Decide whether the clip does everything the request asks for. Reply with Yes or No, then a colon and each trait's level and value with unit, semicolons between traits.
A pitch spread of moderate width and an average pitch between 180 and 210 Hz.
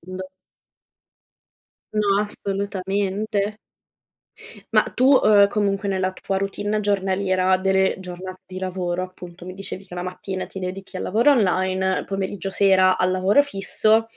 No: narrow, 1.4 semitones; high, 190 Hz